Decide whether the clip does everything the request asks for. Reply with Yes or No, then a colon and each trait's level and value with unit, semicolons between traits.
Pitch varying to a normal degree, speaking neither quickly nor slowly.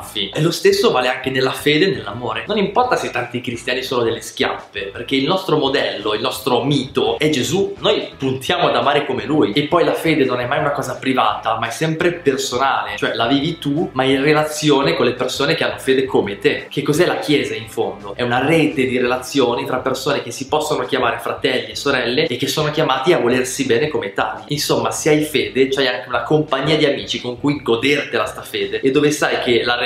No: average, 3.5 semitones; fast, 220 wpm